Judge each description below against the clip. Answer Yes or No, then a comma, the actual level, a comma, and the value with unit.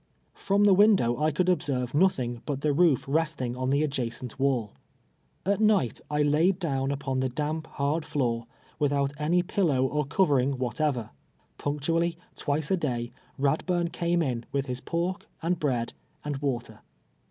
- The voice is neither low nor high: Yes, medium, 145 Hz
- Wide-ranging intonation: No, average, 4.4 semitones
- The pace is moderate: Yes, average, 155 wpm